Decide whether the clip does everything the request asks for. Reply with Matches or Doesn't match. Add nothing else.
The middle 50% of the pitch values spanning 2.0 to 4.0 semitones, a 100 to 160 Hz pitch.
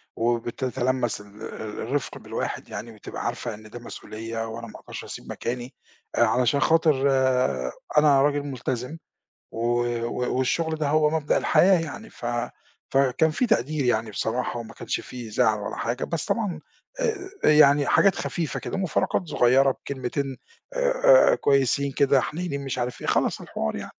Doesn't match